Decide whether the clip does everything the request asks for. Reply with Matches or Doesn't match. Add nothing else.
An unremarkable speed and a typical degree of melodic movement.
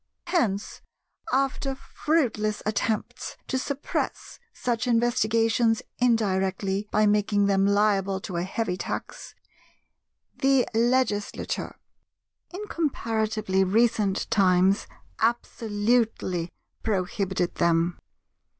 Doesn't match